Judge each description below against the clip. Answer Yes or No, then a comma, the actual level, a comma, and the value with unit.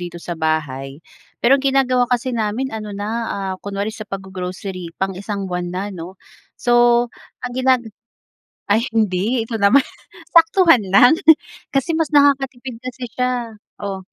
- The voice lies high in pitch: Yes, high, 220 Hz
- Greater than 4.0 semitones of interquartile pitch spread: Yes, average, 4.9 semitones